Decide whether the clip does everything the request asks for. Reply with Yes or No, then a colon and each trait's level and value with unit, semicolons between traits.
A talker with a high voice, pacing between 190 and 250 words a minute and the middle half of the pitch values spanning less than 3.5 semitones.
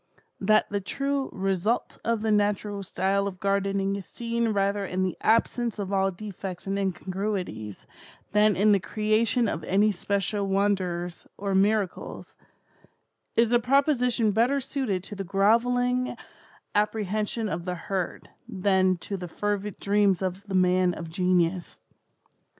No: high, 200 Hz; average, 140 wpm; narrow, 2.4 semitones